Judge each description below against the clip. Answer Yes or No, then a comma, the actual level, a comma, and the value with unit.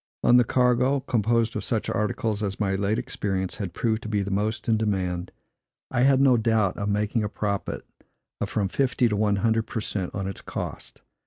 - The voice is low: Yes, low, 110 Hz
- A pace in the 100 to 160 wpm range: No, average, 195 wpm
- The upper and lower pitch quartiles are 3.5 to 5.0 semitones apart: No, average, 2.7 semitones